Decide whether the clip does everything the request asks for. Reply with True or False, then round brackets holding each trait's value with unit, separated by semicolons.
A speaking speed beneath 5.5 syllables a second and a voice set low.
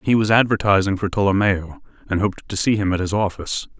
False (6.3 syllables/s; 100 Hz)